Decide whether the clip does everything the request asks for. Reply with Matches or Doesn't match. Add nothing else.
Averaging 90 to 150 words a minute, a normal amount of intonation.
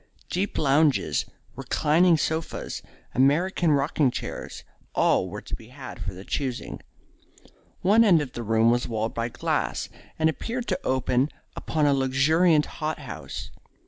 Matches